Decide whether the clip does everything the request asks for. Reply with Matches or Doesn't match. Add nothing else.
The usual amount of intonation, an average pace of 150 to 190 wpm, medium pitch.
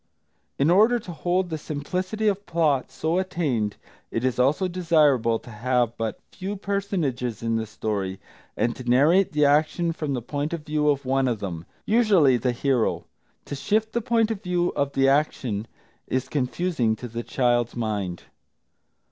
Doesn't match